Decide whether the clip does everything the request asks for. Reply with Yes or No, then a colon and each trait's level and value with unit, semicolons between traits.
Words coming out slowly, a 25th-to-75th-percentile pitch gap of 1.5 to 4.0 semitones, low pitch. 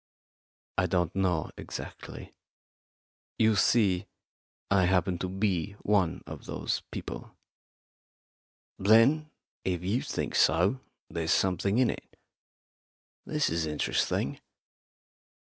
Yes: slow, 100 wpm; average, 3.2 semitones; very low, 95 Hz